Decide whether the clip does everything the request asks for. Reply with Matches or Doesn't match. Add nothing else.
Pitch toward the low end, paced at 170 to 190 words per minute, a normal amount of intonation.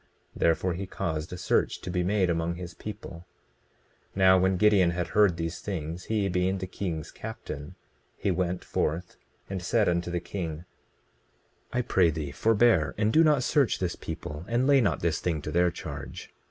Matches